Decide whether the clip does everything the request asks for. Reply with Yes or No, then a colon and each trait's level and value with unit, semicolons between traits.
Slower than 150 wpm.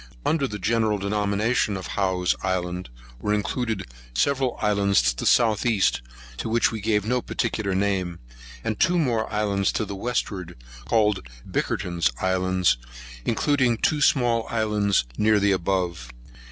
Yes: average, 140 wpm